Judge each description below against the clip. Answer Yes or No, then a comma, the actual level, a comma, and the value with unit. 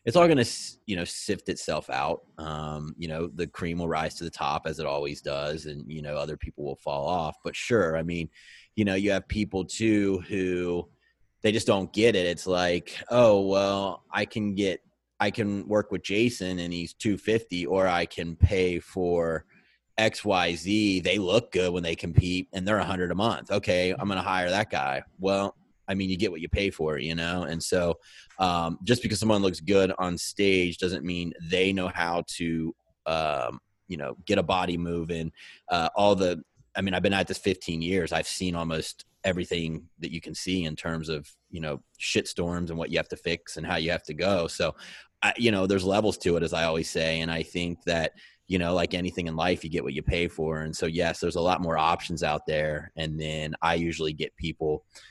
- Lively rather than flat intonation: No, average, 2.9 semitones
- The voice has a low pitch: Yes, very low, 90 Hz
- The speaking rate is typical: No, fast, 225 wpm